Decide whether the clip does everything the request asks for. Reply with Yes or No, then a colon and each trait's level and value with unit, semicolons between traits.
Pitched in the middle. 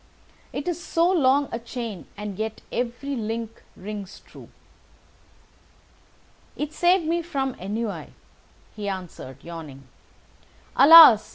No: high, 230 Hz